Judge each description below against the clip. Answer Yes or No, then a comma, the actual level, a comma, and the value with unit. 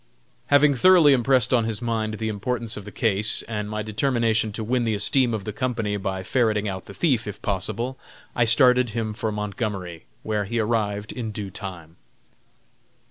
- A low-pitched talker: Yes, low, 110 Hz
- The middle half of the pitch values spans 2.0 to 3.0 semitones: Yes, average, 2.7 semitones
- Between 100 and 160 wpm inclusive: No, average, 180 wpm